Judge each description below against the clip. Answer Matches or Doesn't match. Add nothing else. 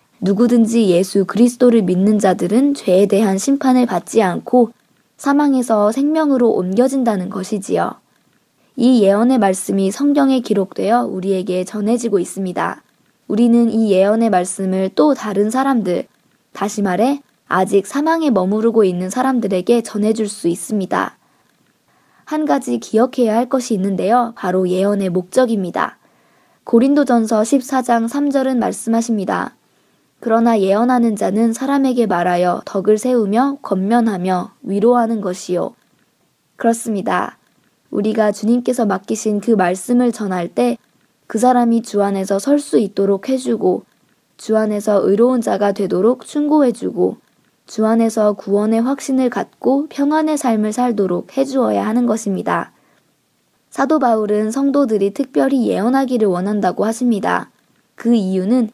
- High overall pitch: Matches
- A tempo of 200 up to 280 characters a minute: Doesn't match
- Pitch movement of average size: Matches